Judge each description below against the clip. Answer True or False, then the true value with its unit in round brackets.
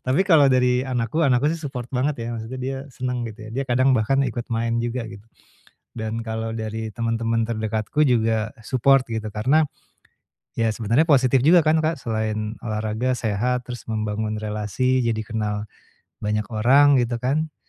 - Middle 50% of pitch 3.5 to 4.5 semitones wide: False (2.9 semitones)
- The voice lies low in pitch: True (115 Hz)